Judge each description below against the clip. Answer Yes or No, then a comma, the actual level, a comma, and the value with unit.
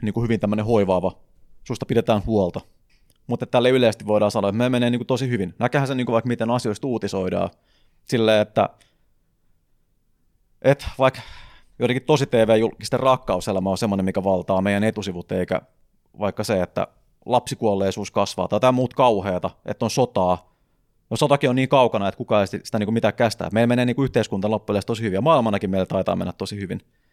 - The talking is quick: Yes, fast, 180 wpm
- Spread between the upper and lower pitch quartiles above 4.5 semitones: No, average, 3.9 semitones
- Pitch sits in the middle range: No, low, 110 Hz